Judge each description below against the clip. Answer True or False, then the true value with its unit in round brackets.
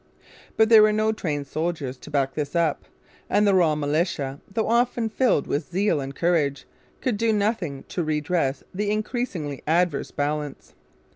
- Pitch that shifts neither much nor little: False (6.5 semitones)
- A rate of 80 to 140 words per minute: False (160 wpm)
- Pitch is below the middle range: False (170 Hz)